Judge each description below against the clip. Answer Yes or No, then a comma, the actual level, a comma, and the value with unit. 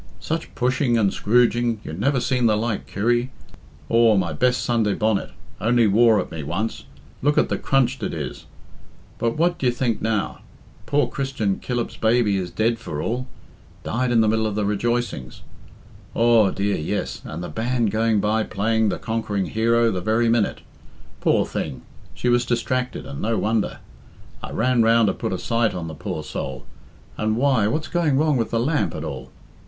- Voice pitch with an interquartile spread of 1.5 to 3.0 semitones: Yes, narrow, 2.6 semitones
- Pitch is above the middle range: No, low, 115 Hz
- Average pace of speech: Yes, average, 180 wpm